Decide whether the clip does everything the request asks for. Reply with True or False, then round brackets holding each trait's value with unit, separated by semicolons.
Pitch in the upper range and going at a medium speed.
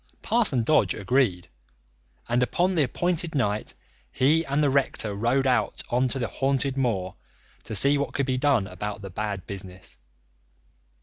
False (130 Hz; 160 wpm)